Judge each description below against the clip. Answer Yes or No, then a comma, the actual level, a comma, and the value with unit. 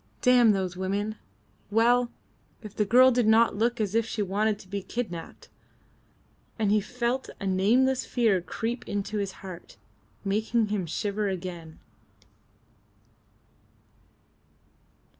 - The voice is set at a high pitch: Yes, high, 210 Hz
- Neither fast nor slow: No, slow, 120 wpm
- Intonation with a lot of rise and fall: No, average, 3.4 semitones